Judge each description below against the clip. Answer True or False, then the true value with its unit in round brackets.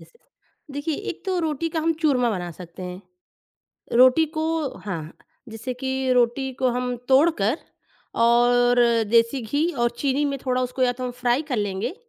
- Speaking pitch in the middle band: False (250 Hz)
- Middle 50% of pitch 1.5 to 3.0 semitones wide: False (3.4 semitones)